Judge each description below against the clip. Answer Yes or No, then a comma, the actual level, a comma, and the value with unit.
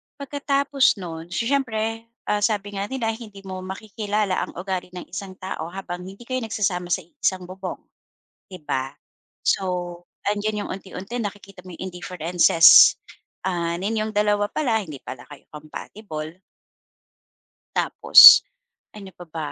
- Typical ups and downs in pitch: Yes, average, 3.4 semitones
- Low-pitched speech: No, high, 195 Hz